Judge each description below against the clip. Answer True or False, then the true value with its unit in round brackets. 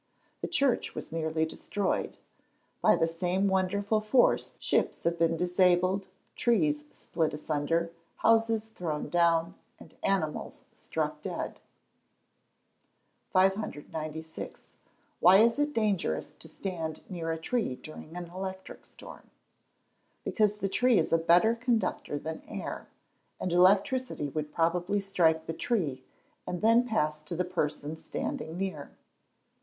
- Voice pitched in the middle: True (180 Hz)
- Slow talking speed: True (125 wpm)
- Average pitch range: True (4.2 semitones)